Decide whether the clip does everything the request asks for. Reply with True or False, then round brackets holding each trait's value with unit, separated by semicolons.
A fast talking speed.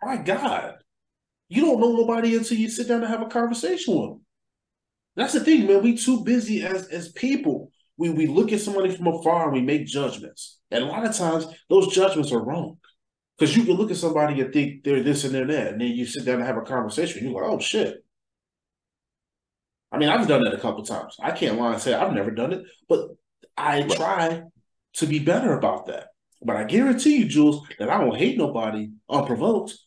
True (220 wpm)